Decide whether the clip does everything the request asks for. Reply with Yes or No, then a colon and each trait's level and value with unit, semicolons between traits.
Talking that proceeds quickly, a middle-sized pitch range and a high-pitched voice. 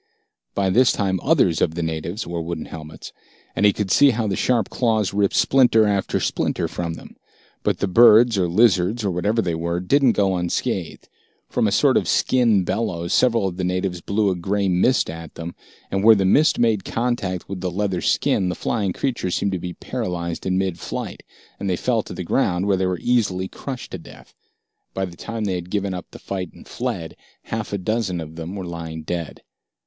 No: fast, 210 wpm; average, 3.9 semitones; very low, 95 Hz